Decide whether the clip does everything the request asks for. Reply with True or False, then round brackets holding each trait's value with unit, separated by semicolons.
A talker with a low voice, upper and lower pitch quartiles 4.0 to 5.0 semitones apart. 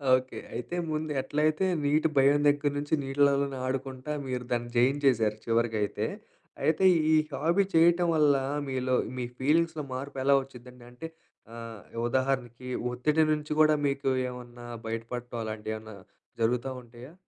False (130 Hz; 3.5 semitones)